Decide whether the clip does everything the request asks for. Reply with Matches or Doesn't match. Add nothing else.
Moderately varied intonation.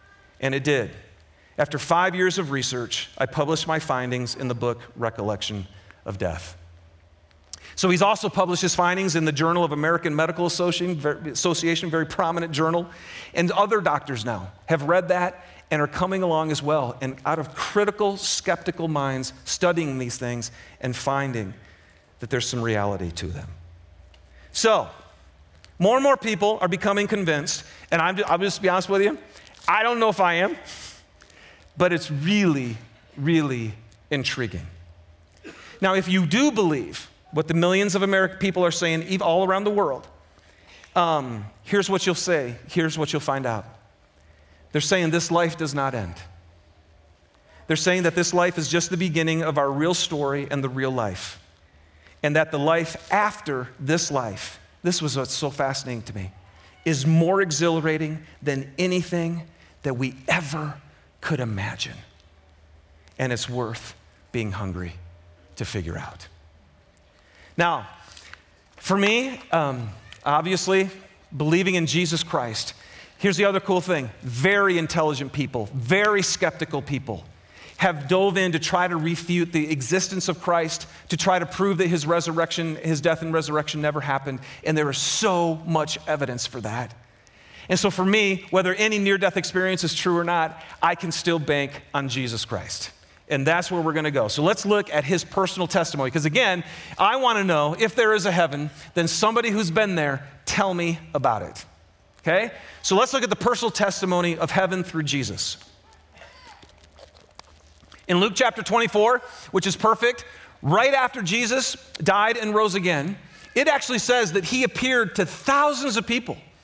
Doesn't match